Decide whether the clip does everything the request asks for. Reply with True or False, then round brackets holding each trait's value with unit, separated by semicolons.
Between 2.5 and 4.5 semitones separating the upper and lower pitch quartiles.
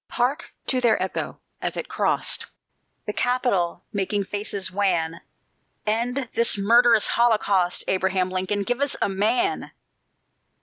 True (4.2 semitones)